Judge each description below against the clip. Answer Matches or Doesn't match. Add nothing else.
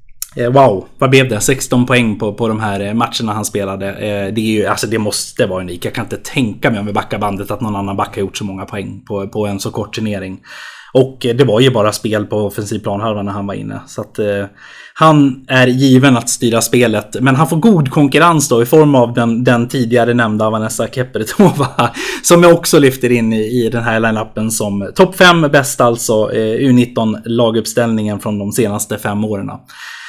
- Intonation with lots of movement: Doesn't match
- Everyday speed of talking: Doesn't match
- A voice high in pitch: Doesn't match